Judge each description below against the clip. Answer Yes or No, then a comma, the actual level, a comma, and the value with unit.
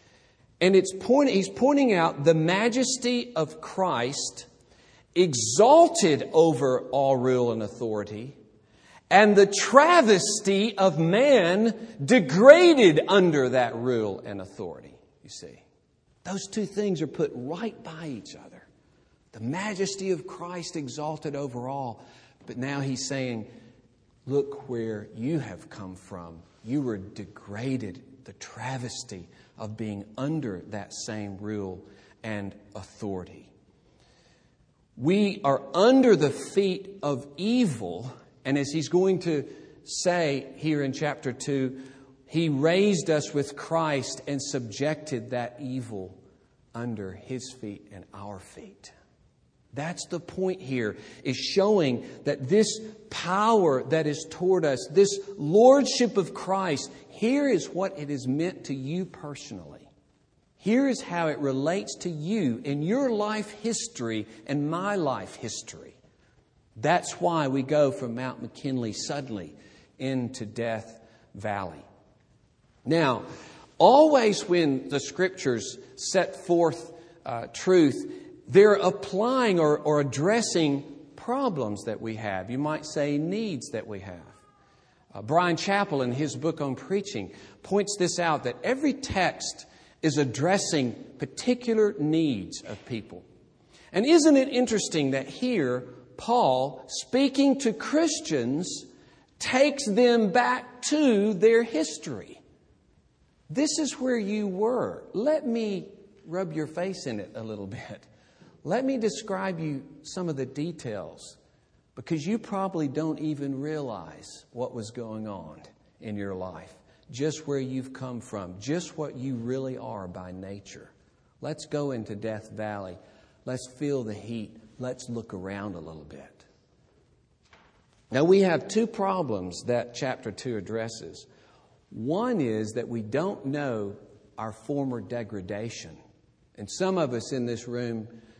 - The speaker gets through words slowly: Yes, slow, 130 wpm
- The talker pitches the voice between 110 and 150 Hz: Yes, medium, 140 Hz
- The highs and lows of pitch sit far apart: Yes, wide, 8.5 semitones